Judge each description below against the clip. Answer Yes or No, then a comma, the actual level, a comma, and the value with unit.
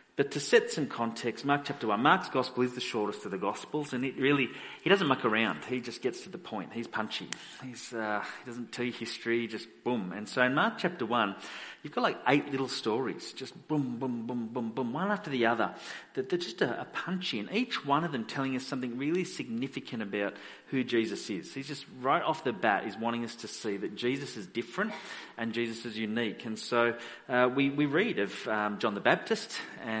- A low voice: Yes, low, 125 Hz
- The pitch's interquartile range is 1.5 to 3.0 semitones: No, average, 3.4 semitones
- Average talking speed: No, fast, 220 wpm